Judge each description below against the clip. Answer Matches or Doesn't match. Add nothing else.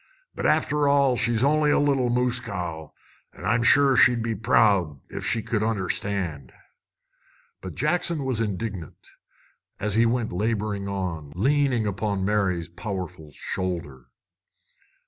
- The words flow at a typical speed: Doesn't match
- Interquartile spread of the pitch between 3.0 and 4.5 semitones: Doesn't match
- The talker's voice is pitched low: Matches